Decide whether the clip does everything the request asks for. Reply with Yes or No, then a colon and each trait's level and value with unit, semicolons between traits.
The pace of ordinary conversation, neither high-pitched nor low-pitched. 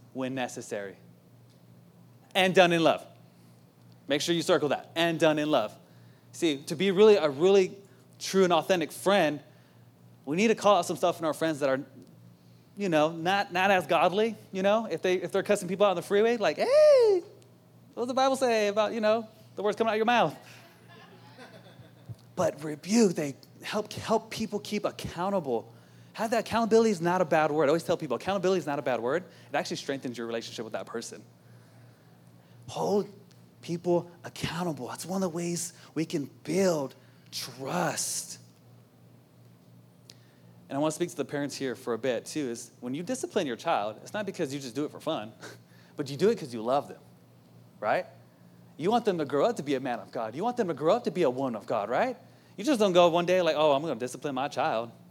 No: fast, 210 wpm; medium, 160 Hz